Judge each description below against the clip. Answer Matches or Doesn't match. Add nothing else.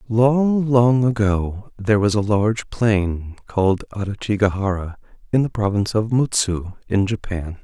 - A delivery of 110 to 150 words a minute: Matches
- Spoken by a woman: Doesn't match